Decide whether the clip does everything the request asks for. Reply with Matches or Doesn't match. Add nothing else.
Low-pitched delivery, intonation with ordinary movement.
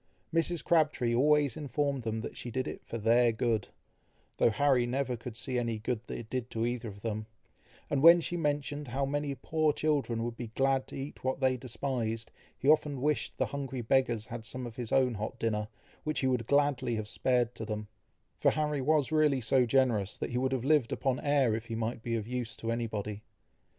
Matches